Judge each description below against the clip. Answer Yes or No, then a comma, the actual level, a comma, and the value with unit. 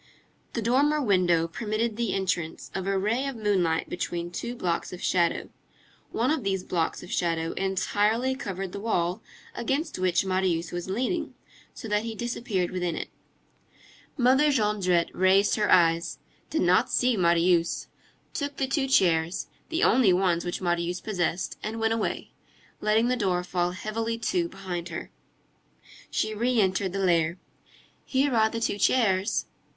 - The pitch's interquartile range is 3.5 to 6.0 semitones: Yes, average, 4.7 semitones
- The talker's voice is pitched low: No, high, 195 Hz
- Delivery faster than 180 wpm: No, average, 155 wpm